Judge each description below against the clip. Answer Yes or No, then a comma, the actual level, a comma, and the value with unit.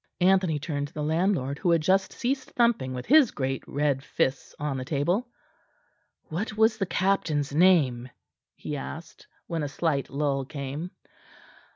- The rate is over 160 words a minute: No, average, 155 wpm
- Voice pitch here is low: No, medium, 155 Hz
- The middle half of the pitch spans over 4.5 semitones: Yes, average, 5.3 semitones